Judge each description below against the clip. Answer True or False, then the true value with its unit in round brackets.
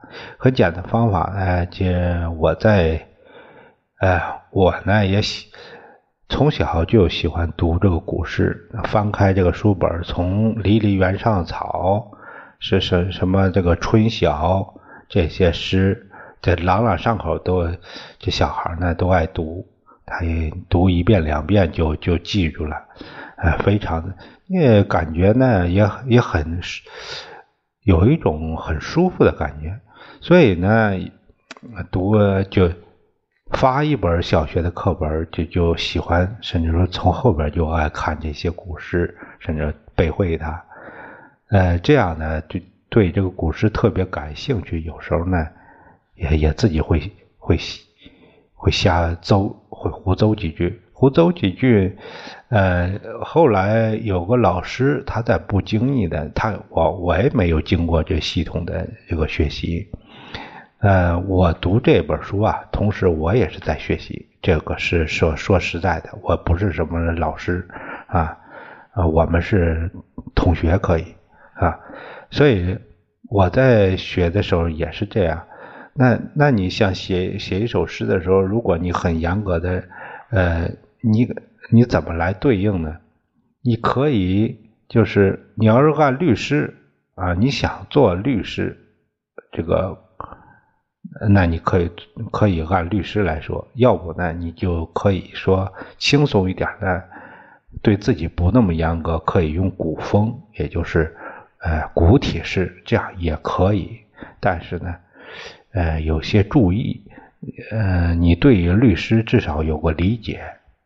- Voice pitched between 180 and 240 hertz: False (95 Hz)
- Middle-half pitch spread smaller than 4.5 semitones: True (4.0 semitones)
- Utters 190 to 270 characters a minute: True (195 characters per minute)